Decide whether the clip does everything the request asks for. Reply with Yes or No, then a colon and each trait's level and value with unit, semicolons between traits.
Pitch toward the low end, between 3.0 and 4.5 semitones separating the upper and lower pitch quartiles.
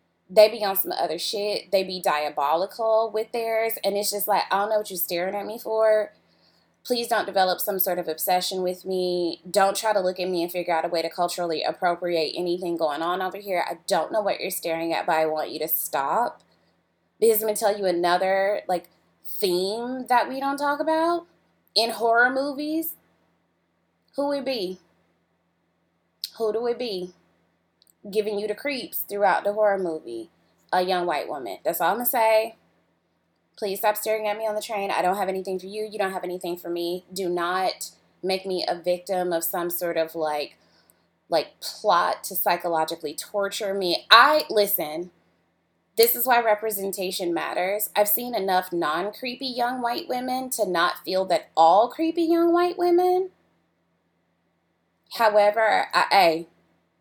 No: high, 195 Hz; average, 4.2 semitones